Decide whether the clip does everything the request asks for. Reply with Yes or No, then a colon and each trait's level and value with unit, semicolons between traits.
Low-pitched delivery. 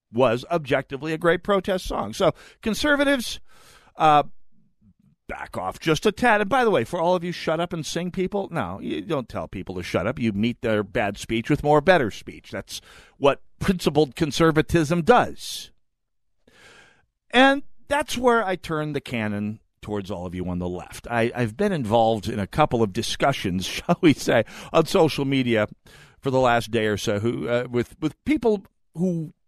No: medium, 150 Hz